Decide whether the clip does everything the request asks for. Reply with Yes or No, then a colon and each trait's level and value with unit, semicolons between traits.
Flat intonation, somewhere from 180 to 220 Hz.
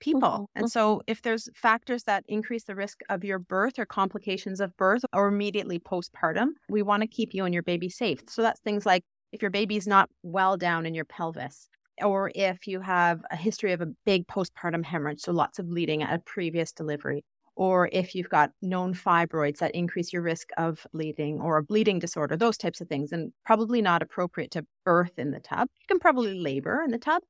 No: average, 3.9 semitones; high, 190 Hz